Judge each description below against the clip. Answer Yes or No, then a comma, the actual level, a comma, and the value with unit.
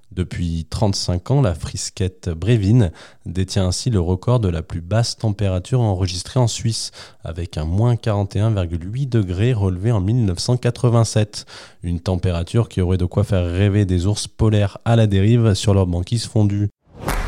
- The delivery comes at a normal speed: Yes, average, 155 wpm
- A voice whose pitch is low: Yes, low, 105 Hz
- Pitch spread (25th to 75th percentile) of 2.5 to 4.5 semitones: Yes, average, 4.1 semitones